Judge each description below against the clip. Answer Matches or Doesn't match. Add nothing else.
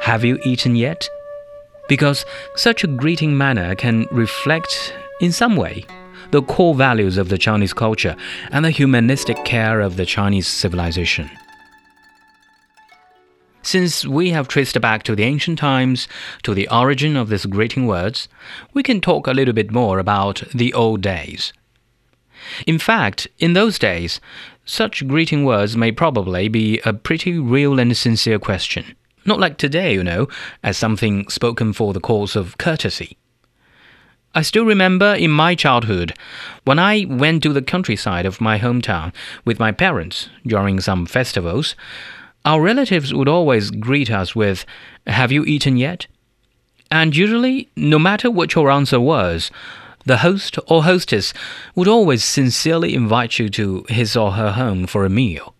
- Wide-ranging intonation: Matches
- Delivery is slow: Doesn't match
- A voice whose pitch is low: Matches